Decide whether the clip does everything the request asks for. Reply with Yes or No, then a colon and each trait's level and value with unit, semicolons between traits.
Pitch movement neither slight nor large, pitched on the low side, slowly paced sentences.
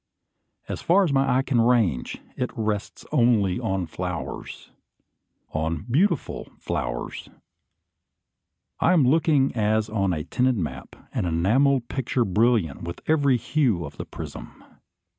No: wide, 6.0 semitones; low, 115 Hz; slow, 130 wpm